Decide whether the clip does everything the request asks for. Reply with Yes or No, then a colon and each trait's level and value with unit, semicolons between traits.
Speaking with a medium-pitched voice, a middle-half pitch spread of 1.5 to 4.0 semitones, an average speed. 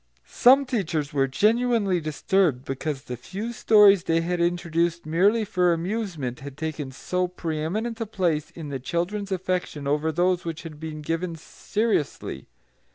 No: medium, 170 Hz; average, 4.5 semitones; average, 160 wpm